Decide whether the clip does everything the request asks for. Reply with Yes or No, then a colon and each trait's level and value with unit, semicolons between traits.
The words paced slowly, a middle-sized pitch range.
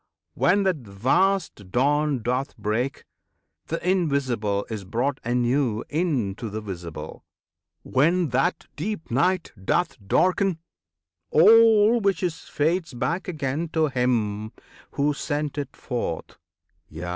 No: slow, 115 wpm; wide, 7.2 semitones